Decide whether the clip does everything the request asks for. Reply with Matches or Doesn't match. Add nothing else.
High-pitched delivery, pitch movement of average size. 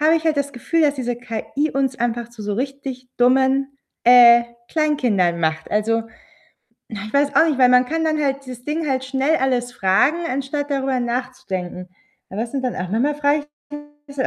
Matches